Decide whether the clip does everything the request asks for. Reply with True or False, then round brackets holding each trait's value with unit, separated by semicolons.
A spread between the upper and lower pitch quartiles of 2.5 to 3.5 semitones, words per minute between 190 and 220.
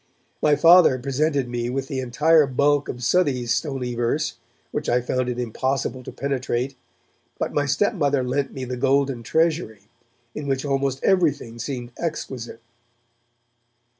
False (2.9 semitones; 140 wpm)